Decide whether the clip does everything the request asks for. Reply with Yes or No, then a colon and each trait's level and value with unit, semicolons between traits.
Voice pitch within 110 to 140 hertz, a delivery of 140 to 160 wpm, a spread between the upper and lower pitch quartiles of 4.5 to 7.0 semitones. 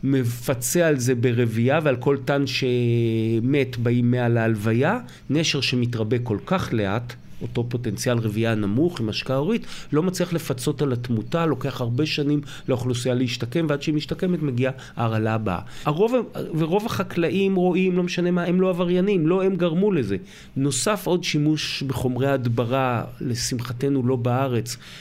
Yes: low, 135 Hz; average, 145 wpm; average, 5.2 semitones